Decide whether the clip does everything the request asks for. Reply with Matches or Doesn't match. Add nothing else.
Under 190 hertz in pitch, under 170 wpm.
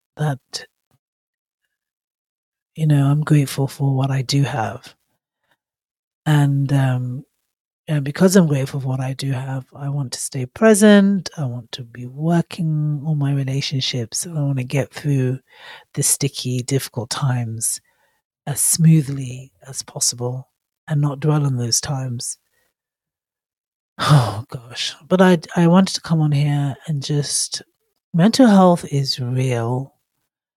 Matches